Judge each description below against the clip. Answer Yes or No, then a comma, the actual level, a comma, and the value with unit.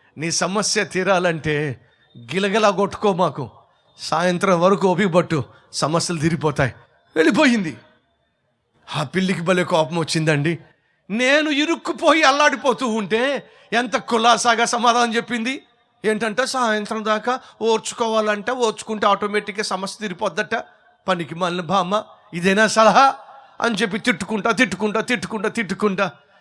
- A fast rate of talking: No, average, 100 wpm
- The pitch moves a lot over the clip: No, average, 4.4 semitones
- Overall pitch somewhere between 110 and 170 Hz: No, high, 215 Hz